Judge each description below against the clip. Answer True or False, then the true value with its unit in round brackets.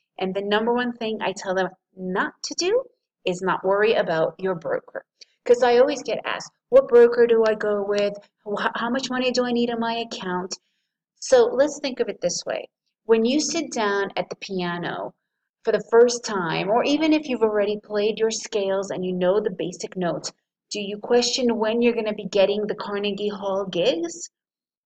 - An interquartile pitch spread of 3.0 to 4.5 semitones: True (3.7 semitones)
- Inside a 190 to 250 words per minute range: True (200 wpm)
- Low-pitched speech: False (220 Hz)